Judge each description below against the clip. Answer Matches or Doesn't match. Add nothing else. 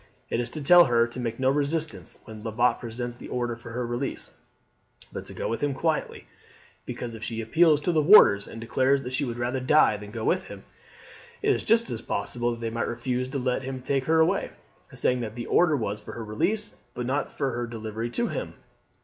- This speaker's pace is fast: Matches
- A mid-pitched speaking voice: Doesn't match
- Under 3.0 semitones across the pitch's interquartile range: Doesn't match